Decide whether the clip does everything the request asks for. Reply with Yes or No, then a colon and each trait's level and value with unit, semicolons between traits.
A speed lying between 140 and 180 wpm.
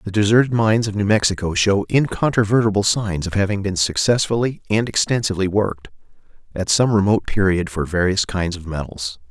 Yes: average, 160 wpm